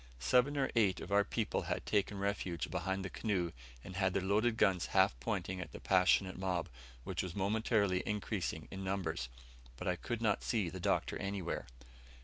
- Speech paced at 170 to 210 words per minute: Yes, average, 180 wpm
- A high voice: No, very low, 95 Hz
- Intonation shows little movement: Yes, narrow, 2.2 semitones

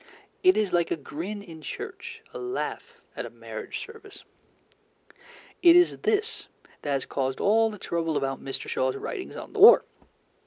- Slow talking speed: No, average, 165 wpm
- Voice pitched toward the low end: No, high, 205 Hz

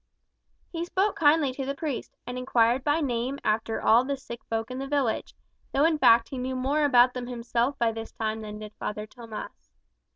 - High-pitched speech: Yes, very high, 250 Hz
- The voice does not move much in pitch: No, average, 3.5 semitones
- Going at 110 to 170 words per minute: No, average, 200 wpm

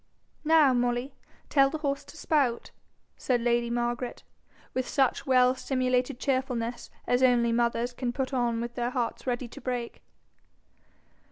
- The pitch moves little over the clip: Yes, narrow, 1.7 semitones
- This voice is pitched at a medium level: No, very high, 250 Hz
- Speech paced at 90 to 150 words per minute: Yes, average, 140 wpm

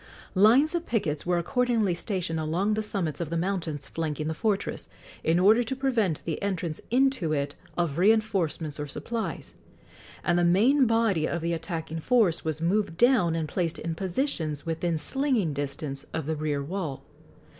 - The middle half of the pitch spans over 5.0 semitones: Yes, wide, 5.4 semitones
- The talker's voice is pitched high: No, medium, 175 Hz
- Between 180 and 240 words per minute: No, average, 165 wpm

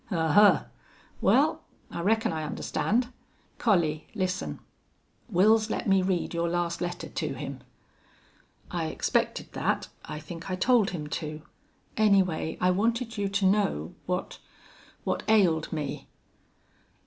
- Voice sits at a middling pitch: Yes, medium, 180 Hz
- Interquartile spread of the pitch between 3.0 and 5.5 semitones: Yes, average, 4.3 semitones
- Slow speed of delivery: Yes, slow, 125 wpm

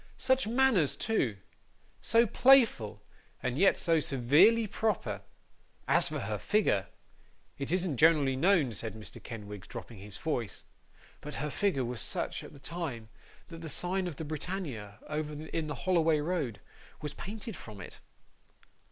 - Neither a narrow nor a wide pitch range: No, wide, 7.7 semitones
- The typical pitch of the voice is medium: Yes, medium, 155 Hz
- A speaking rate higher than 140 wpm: Yes, average, 150 wpm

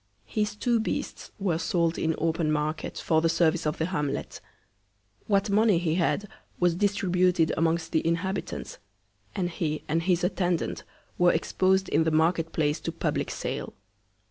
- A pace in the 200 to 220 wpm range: No, average, 155 wpm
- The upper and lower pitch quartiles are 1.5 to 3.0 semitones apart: Yes, narrow, 2.5 semitones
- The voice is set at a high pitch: No, medium, 170 Hz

